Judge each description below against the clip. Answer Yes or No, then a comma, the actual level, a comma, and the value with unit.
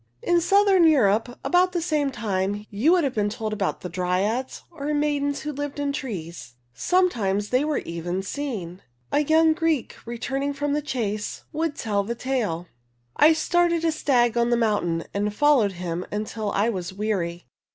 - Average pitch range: No, wide, 6.9 semitones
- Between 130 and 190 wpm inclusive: Yes, average, 175 wpm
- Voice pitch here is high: Yes, high, 235 Hz